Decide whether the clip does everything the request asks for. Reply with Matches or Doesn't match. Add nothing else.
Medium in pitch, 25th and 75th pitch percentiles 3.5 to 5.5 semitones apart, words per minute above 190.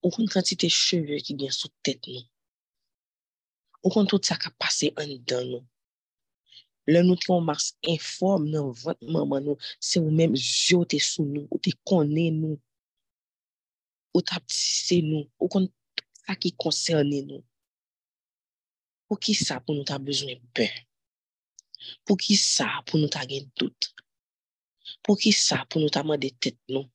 Doesn't match